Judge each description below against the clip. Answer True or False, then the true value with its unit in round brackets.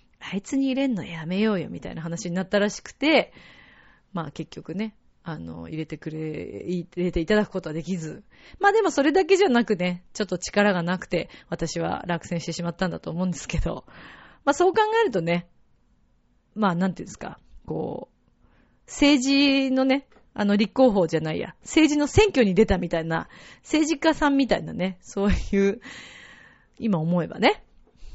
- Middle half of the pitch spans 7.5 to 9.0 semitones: True (7.8 semitones)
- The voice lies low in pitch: False (195 Hz)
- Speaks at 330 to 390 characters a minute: True (340 characters per minute)